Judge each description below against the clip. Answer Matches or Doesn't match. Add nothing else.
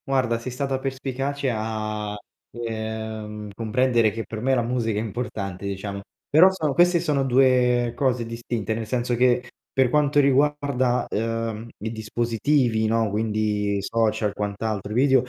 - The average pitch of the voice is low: Matches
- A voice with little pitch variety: Doesn't match